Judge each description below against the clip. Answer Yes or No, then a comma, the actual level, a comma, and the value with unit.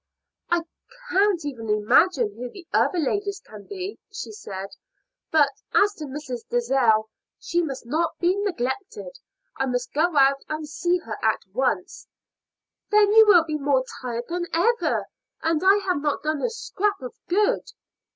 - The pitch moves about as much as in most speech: No, wide, 7.0 semitones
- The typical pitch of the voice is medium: No, very high, 315 Hz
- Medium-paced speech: Yes, average, 160 wpm